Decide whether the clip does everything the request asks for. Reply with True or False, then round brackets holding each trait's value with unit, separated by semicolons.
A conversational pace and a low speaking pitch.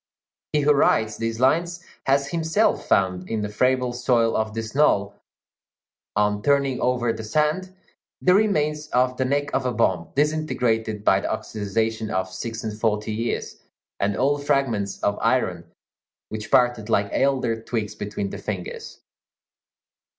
True (150 wpm; 115 Hz)